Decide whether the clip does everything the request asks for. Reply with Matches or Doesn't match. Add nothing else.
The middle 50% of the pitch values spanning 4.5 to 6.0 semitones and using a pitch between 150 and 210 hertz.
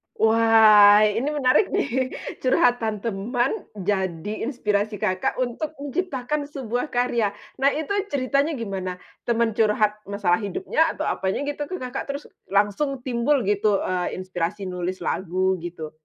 Doesn't match